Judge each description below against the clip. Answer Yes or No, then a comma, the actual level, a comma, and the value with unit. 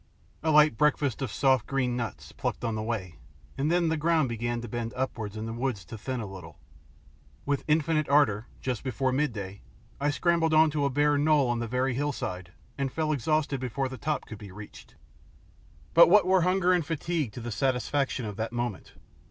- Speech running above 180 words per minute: Yes, average, 200 wpm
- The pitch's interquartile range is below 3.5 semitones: No, average, 4.6 semitones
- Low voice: Yes, low, 130 Hz